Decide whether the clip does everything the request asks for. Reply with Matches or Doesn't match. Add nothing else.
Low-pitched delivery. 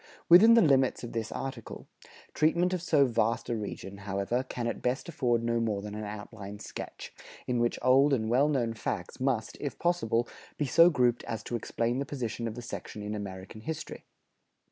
Matches